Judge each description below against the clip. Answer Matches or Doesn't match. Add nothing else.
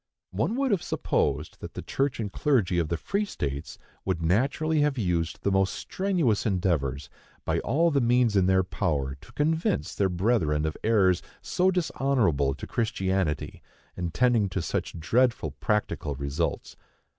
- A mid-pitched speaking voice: Doesn't match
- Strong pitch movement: Matches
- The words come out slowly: Doesn't match